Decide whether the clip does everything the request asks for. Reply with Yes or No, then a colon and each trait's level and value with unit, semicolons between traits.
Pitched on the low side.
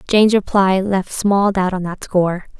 No: high, 190 Hz